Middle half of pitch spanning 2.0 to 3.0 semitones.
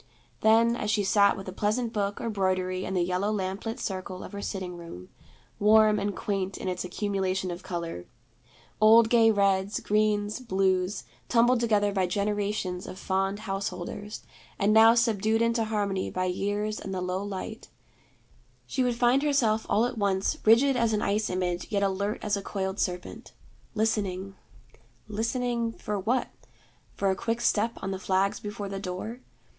Yes: narrow, 2.6 semitones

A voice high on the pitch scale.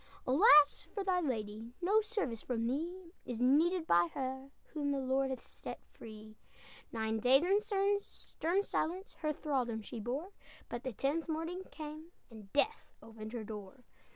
Yes: very high, 275 Hz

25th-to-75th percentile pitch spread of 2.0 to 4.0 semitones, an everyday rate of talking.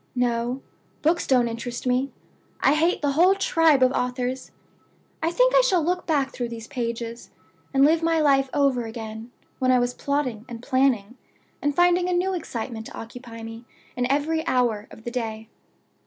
No: average, 4.6 semitones; average, 180 wpm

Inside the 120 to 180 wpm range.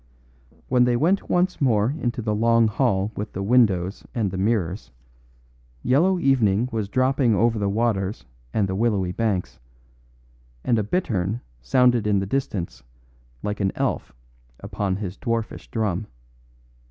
Yes: average, 140 wpm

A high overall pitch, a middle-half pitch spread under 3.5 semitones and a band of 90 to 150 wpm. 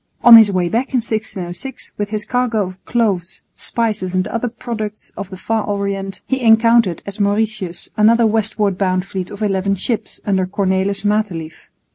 No: high, 205 Hz; average, 2.8 semitones; average, 165 wpm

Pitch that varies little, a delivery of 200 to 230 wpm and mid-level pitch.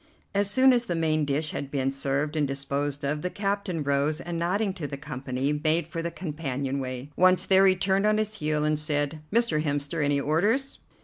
No: average, 4.8 semitones; fast, 205 wpm; medium, 155 Hz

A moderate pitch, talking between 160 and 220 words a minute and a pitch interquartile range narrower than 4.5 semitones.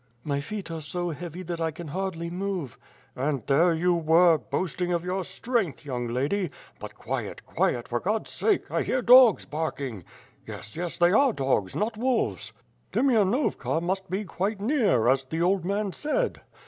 No: medium, 175 Hz; average, 170 wpm; average, 4.9 semitones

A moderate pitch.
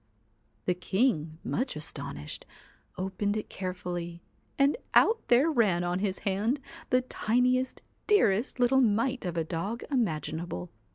No: high, 200 Hz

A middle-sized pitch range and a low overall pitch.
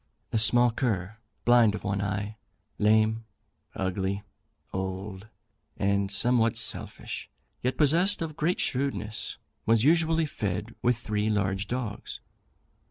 Yes: average, 3.7 semitones; low, 110 Hz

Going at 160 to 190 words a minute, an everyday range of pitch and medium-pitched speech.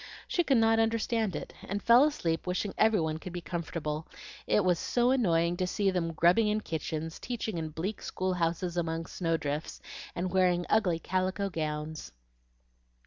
Yes: average, 170 wpm; average, 4.3 semitones; medium, 180 Hz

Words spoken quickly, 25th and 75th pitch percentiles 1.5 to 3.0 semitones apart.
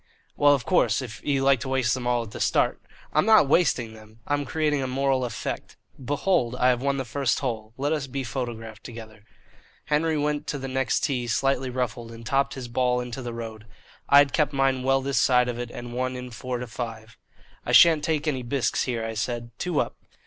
Yes: fast, 220 wpm; average, 2.7 semitones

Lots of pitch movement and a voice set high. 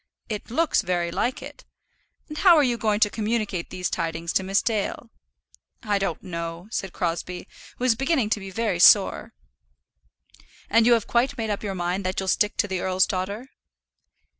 No: average, 4.0 semitones; high, 205 Hz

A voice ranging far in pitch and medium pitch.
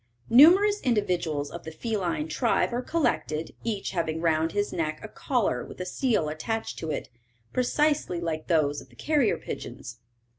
Yes: wide, 7.4 semitones; medium, 175 Hz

